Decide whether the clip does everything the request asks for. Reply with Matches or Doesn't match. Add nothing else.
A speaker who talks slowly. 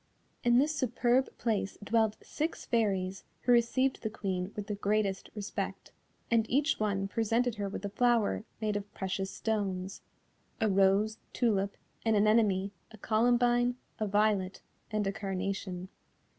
Doesn't match